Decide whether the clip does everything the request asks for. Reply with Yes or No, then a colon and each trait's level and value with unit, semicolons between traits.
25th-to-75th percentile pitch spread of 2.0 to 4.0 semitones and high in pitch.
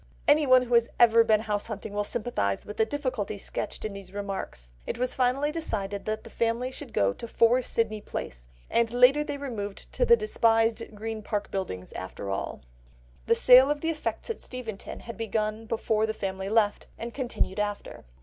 Yes: average, 3.4 semitones; high, 225 Hz